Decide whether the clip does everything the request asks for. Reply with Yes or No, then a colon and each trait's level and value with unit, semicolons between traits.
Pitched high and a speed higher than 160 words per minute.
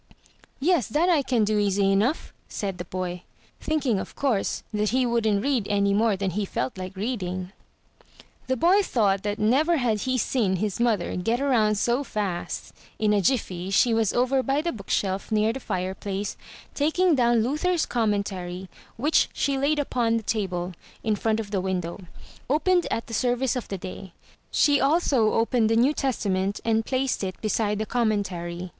Yes: high, 220 Hz; average, 180 wpm